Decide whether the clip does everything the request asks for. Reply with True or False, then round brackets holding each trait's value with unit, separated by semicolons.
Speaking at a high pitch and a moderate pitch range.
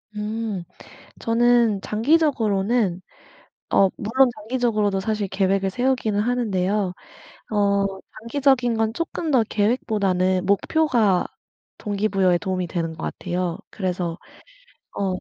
True (210 Hz; 3.7 semitones)